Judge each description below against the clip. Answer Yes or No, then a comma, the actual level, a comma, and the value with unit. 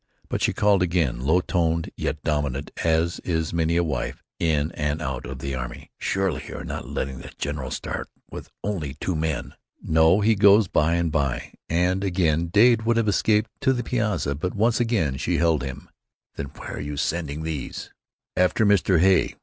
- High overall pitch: No, very low, 85 Hz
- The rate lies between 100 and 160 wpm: No, average, 190 wpm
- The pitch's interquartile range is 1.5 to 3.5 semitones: No, average, 4.7 semitones